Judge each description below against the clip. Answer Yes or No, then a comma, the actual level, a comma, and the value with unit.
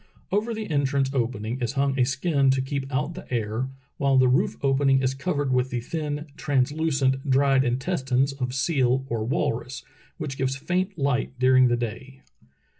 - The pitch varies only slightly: Yes, narrow, 1.9 semitones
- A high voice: No, low, 135 Hz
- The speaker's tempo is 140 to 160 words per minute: No, average, 175 wpm